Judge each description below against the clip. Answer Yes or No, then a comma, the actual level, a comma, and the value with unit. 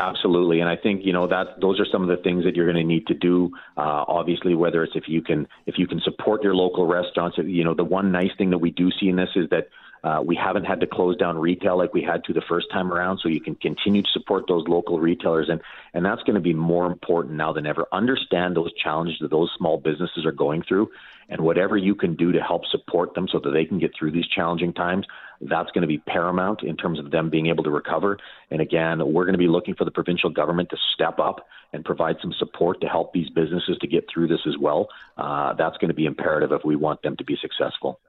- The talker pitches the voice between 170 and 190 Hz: No, very low, 85 Hz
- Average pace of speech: No, fast, 260 wpm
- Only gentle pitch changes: Yes, narrow, 1.5 semitones